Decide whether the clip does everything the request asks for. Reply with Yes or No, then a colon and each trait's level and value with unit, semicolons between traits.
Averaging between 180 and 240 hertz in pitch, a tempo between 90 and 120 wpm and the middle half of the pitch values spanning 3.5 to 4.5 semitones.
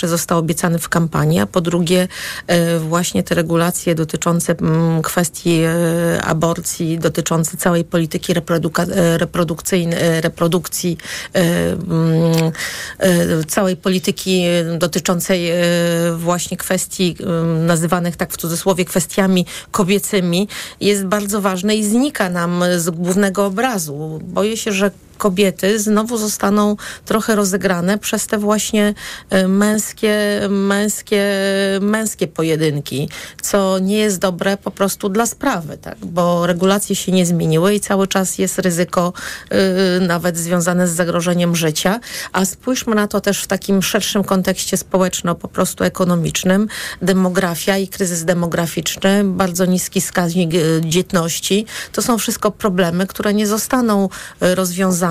No: medium, 185 Hz; average, 115 wpm; average, 2.7 semitones